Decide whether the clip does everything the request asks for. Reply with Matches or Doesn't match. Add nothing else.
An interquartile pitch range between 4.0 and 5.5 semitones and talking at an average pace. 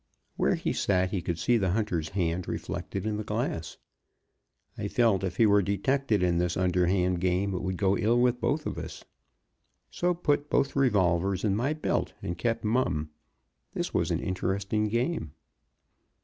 Matches